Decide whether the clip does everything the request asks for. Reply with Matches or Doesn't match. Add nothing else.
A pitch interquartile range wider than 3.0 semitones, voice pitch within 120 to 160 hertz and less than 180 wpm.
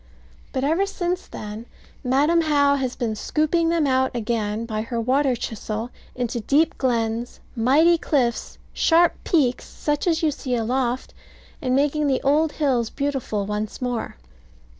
Doesn't match